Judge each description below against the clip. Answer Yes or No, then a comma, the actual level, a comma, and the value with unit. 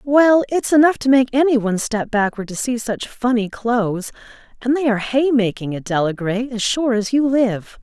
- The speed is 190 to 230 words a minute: Yes, average, 200 wpm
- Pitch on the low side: No, high, 235 Hz